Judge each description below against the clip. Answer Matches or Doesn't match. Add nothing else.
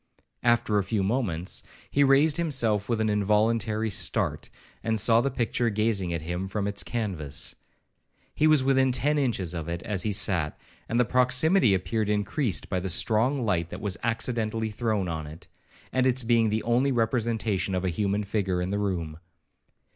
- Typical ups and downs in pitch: Matches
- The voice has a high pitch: Doesn't match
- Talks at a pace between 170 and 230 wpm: Matches